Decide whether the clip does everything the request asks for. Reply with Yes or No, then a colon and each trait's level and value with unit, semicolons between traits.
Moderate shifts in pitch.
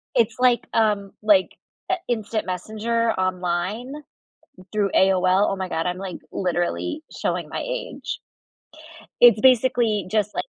Yes: average, 4.1 semitones